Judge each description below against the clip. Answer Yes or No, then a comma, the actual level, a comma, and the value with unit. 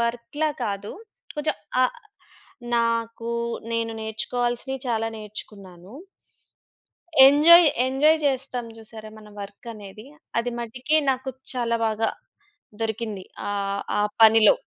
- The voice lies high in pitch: Yes, high, 230 Hz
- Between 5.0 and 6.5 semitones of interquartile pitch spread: No, average, 2.8 semitones